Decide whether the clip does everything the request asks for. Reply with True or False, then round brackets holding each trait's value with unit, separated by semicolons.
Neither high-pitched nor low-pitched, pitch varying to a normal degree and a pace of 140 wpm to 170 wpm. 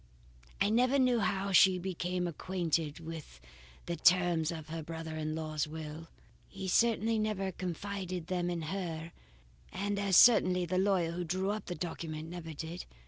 True (175 Hz; 3.0 semitones; 160 wpm)